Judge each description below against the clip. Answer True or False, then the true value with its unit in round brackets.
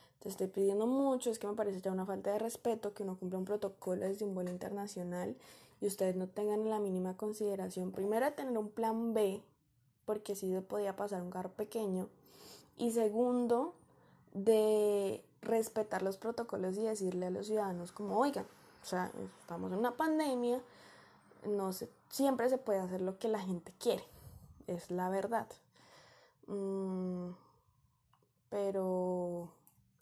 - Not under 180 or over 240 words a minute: False (155 wpm)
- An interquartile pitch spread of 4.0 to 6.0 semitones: False (2.9 semitones)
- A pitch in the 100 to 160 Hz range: False (200 Hz)